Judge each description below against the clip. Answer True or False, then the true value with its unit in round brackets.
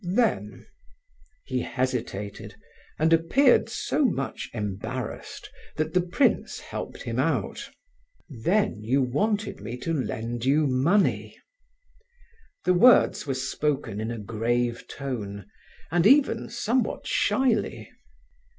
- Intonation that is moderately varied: False (7.5 semitones)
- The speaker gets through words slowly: True (110 wpm)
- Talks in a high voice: False (135 Hz)